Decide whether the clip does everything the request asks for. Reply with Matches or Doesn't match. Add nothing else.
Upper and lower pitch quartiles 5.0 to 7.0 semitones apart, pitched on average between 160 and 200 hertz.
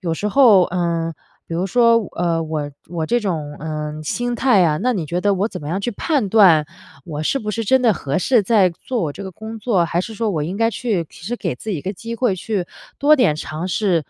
Matches